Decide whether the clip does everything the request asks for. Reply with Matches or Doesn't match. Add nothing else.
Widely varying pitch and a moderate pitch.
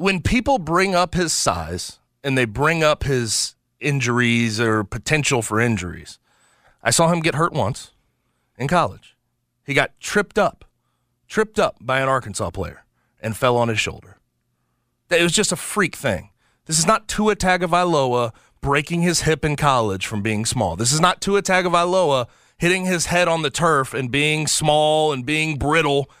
Matches